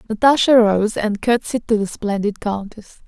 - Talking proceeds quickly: No, average, 155 wpm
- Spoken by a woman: Yes, female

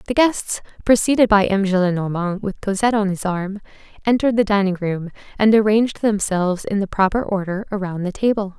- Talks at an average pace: Yes, average, 175 wpm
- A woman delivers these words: Yes, female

